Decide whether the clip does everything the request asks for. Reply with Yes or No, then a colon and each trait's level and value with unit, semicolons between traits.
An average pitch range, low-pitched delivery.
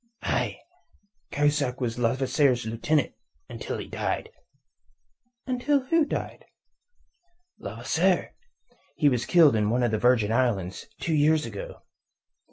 Yes: average, 4.9 semitones; low, 130 Hz